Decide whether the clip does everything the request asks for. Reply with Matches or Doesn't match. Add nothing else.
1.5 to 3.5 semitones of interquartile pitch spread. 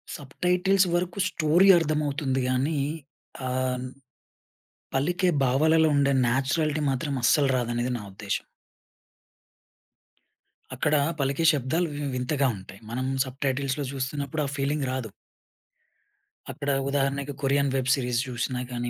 Matches